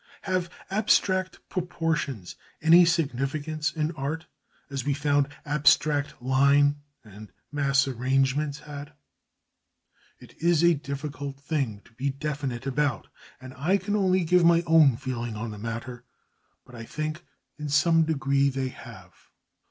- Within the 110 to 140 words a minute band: Yes, slow, 135 wpm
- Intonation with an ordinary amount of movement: Yes, average, 3.4 semitones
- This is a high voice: No, medium, 145 Hz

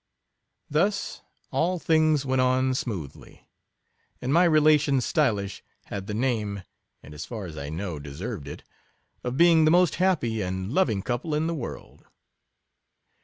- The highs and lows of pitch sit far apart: Yes, wide, 7.8 semitones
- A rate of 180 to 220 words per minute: No, average, 145 wpm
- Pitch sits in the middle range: No, low, 130 Hz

